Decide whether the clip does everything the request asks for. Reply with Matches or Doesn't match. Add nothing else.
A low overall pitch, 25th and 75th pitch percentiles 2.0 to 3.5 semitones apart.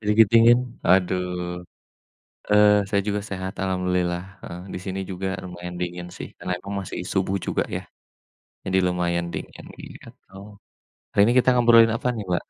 Matches